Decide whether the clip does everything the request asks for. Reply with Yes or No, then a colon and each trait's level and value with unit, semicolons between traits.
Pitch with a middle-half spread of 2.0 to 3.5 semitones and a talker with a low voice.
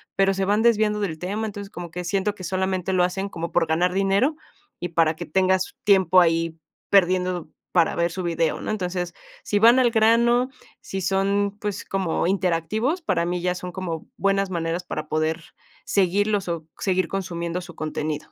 No: average, 2.7 semitones; medium, 185 Hz